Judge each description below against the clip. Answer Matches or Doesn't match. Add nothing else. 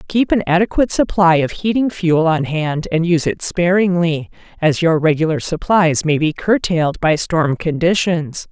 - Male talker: Doesn't match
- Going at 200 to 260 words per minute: Doesn't match